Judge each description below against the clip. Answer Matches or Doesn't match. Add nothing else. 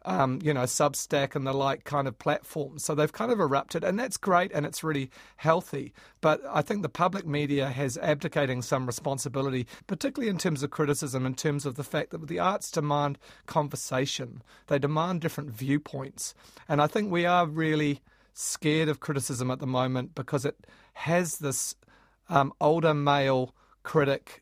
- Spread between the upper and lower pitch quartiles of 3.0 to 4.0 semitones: Doesn't match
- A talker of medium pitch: Matches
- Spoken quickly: Doesn't match